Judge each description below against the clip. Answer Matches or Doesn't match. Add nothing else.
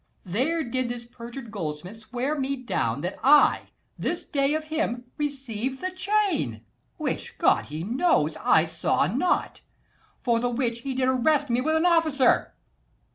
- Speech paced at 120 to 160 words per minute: Matches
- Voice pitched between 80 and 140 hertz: Doesn't match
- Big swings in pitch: Doesn't match